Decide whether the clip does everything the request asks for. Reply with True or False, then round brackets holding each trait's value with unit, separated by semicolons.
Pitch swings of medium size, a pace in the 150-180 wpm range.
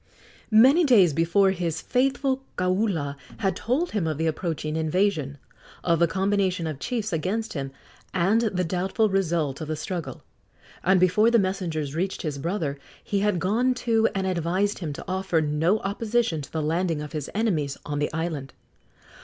True (4.6 semitones; 170 wpm)